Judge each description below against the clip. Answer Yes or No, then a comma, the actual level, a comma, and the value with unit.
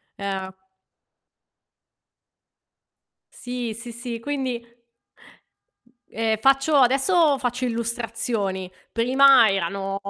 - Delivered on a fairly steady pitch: No, average, 3.3 semitones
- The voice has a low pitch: No, high, 235 Hz